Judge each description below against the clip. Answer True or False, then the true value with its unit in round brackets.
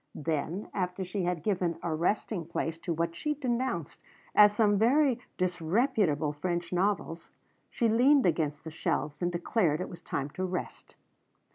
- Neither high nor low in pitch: True (180 Hz)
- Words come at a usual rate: True (155 wpm)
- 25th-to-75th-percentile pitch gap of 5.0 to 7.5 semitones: False (4.4 semitones)